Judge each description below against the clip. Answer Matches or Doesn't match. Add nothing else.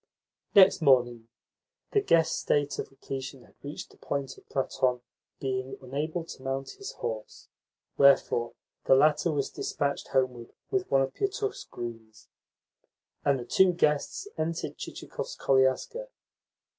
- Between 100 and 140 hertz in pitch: Matches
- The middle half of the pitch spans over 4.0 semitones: Doesn't match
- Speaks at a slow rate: Matches